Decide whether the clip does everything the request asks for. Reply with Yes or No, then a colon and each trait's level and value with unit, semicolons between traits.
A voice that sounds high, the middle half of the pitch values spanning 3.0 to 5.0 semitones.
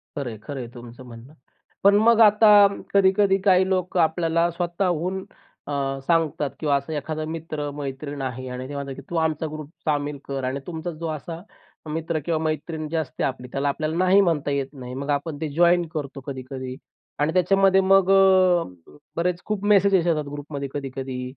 No: medium, 155 Hz; average, 4.2 semitones